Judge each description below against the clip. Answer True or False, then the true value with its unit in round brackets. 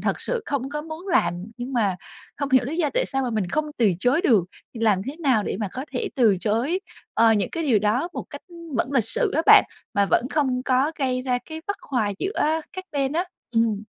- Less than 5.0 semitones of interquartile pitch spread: False (5.6 semitones)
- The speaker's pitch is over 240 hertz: True (260 Hz)